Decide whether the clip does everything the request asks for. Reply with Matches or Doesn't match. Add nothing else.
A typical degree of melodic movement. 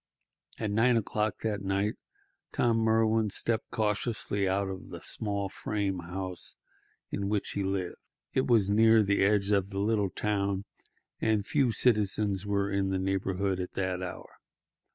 Doesn't match